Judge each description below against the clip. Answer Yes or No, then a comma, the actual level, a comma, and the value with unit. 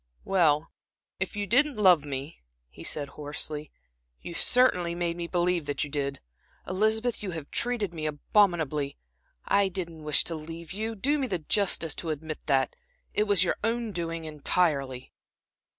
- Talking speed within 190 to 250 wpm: No, average, 160 wpm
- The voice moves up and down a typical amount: Yes, average, 5.0 semitones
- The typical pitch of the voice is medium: Yes, medium, 170 Hz